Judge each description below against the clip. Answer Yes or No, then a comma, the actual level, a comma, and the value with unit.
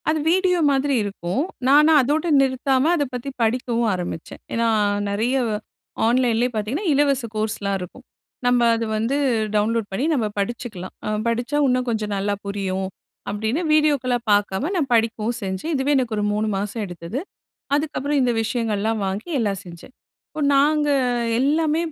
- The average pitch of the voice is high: Yes, high, 235 Hz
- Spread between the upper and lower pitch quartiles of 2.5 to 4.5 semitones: No, average, 5.0 semitones